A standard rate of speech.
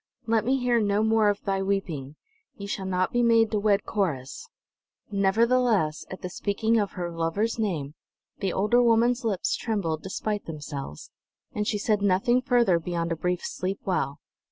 Yes: average, 170 wpm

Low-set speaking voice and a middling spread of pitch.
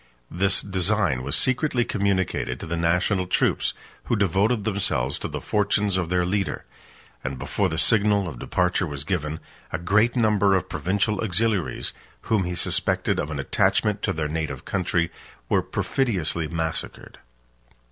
Yes: very low, 95 Hz; average, 4.0 semitones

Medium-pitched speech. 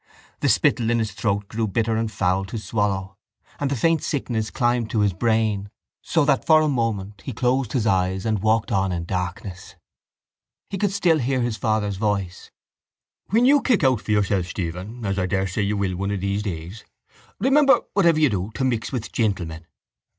No: low, 110 Hz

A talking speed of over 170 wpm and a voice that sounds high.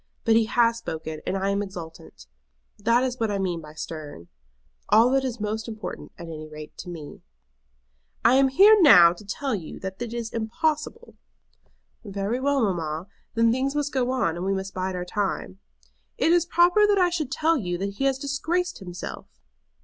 Yes: average, 190 wpm; high, 220 Hz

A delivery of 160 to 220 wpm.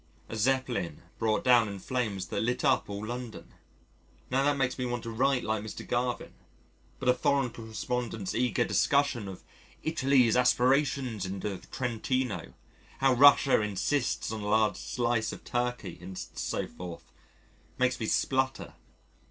No: average, 150 wpm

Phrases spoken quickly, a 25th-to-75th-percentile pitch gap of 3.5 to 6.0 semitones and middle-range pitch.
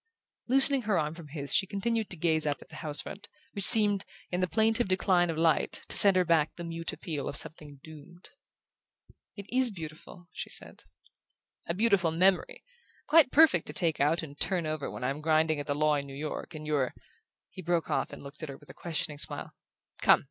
Yes: fast, 215 wpm; average, 4.1 semitones; medium, 165 Hz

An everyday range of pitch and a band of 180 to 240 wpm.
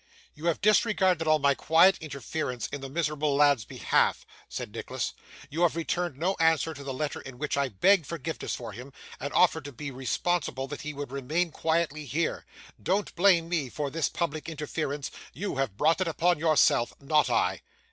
Yes: average, 3.3 semitones; average, 185 wpm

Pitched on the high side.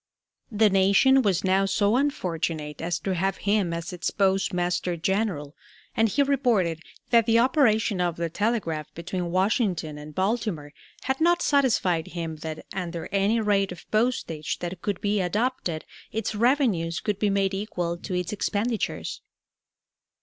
Yes: high, 195 Hz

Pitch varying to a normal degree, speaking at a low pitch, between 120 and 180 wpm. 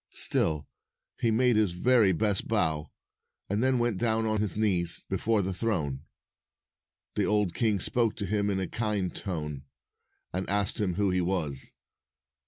Yes: average, 3.7 semitones; low, 100 Hz; average, 160 wpm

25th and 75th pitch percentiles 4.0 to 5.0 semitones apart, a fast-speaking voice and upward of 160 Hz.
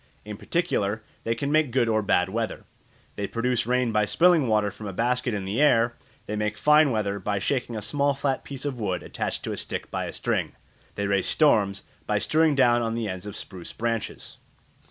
No: average, 4.4 semitones; fast, 210 wpm; low, 115 Hz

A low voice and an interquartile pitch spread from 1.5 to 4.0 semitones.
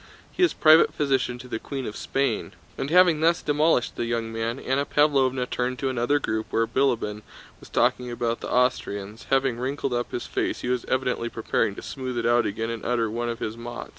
Yes: low, 125 Hz; average, 2.7 semitones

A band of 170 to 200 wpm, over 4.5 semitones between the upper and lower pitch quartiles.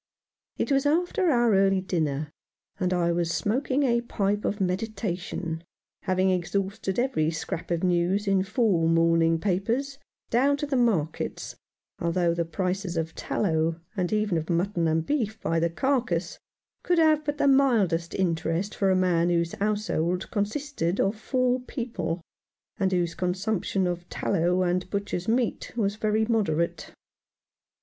No: average, 150 wpm; average, 4.9 semitones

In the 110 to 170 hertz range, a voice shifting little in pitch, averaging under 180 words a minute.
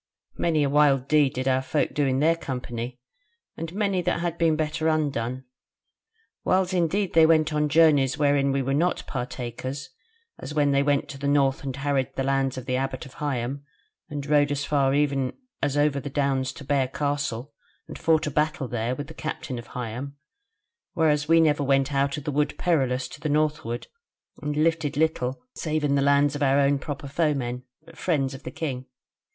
No: medium, 140 Hz; narrow, 2.3 semitones; average, 195 wpm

